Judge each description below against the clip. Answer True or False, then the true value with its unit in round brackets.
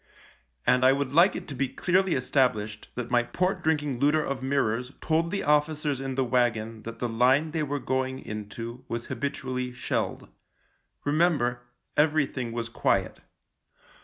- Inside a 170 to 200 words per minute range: False (155 wpm)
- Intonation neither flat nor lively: True (3.5 semitones)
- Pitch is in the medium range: False (130 Hz)